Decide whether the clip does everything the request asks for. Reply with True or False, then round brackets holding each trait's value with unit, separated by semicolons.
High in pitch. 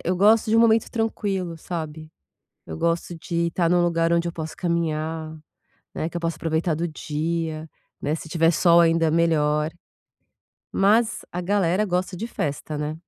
False (170 Hz)